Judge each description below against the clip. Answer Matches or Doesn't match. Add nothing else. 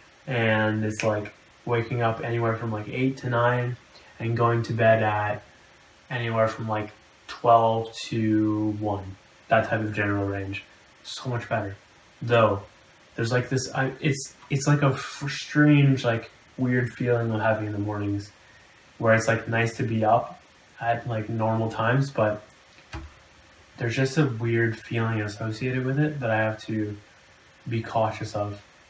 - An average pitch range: Doesn't match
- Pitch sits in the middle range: Doesn't match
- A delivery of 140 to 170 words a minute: Matches